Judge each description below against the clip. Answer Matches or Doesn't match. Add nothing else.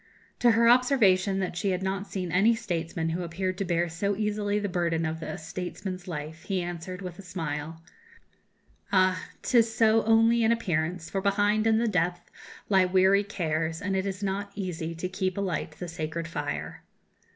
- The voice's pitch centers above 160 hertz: Matches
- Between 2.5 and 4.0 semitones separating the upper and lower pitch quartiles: Matches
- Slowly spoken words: Doesn't match